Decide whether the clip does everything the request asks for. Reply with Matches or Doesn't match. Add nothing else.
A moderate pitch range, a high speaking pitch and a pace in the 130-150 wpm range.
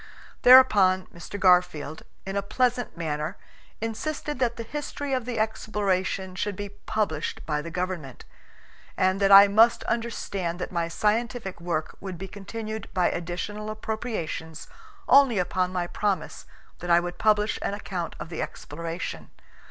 Matches